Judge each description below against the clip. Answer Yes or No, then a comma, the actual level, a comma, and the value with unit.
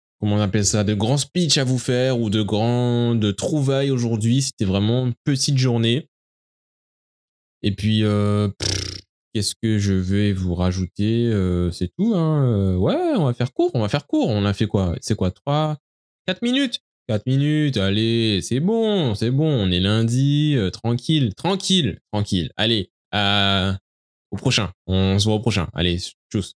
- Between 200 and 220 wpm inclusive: No, average, 180 wpm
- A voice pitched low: Yes, low, 110 Hz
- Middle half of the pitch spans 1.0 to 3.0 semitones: No, wide, 5.4 semitones